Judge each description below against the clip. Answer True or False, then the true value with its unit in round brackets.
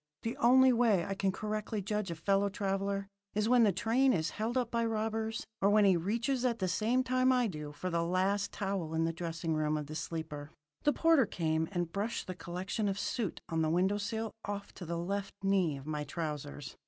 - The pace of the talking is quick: True (215 wpm)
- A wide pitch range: False (4.9 semitones)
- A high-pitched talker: True (195 Hz)